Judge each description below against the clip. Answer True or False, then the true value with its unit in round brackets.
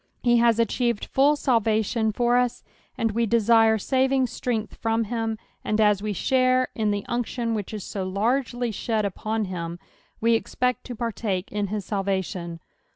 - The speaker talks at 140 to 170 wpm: True (160 wpm)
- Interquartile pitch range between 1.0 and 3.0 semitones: True (2.7 semitones)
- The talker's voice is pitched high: True (225 Hz)